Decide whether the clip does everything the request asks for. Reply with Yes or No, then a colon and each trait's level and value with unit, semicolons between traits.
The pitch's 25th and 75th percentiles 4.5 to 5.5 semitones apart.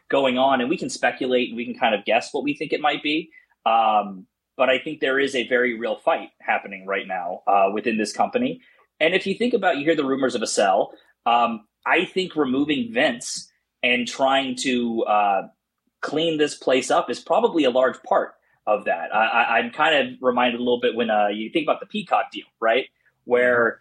Yes: average, 5.1 semitones